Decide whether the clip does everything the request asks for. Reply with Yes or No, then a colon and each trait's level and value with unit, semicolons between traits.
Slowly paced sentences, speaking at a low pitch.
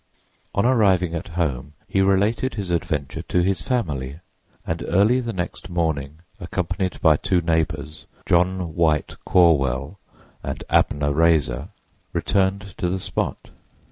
Yes: slow, 130 wpm; very low, 85 Hz